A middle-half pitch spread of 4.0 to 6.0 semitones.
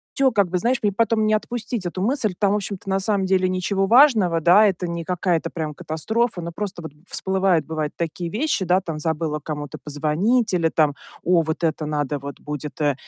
Yes: average, 4.6 semitones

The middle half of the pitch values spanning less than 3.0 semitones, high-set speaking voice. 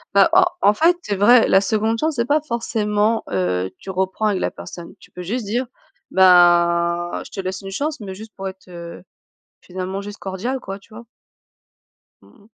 No: average, 3.7 semitones; high, 200 Hz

